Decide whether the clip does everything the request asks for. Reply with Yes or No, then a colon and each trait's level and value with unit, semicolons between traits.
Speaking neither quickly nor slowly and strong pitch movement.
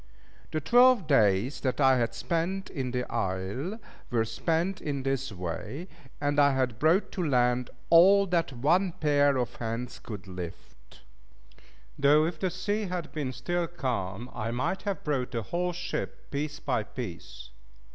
Yes: average, 155 wpm; wide, 6.0 semitones